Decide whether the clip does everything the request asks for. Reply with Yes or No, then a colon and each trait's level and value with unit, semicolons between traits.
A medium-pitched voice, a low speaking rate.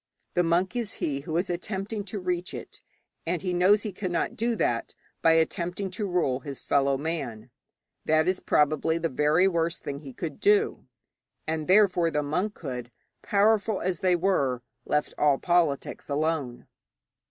No: medium, 170 Hz; average, 165 wpm